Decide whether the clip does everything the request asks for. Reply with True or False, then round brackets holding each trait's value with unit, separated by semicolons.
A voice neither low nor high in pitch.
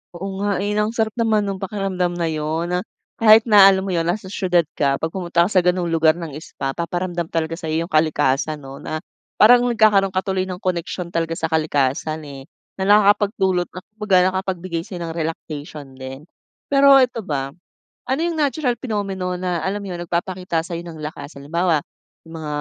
True (180 Hz)